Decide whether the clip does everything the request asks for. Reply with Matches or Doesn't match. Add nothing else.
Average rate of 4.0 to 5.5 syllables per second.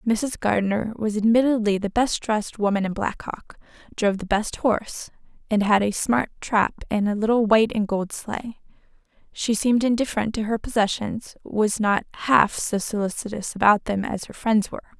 Matches